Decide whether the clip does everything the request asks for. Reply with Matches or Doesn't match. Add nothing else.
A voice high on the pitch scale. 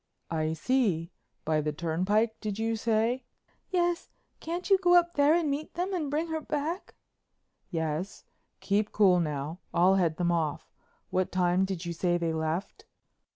Matches